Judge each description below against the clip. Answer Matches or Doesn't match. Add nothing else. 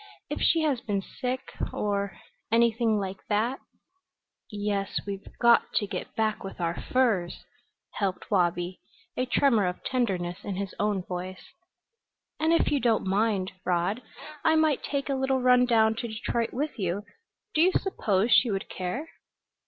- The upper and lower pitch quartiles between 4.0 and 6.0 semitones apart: Matches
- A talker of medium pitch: Doesn't match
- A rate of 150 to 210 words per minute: Matches